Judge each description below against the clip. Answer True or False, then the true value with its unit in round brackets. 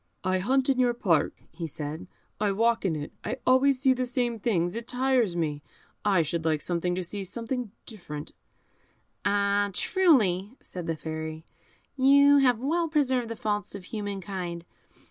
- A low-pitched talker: False (205 Hz)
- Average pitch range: False (6.5 semitones)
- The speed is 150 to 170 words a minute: True (165 wpm)